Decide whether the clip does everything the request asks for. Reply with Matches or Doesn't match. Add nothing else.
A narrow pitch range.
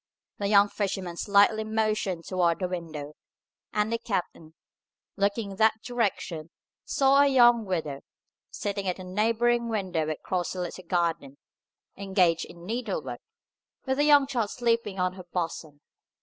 Doesn't match